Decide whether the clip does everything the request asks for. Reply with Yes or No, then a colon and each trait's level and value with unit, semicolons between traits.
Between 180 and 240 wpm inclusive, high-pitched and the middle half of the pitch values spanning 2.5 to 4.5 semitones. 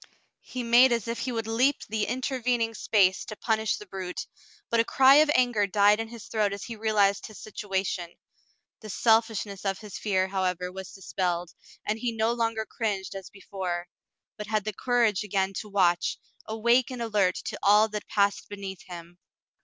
Yes: average, 185 wpm; high, 210 Hz; average, 2.9 semitones